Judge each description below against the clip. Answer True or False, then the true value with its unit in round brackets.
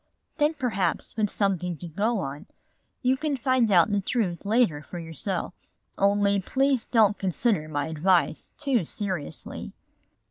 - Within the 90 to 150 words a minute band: True (140 wpm)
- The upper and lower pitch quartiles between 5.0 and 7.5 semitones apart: True (5.6 semitones)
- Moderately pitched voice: False (200 Hz)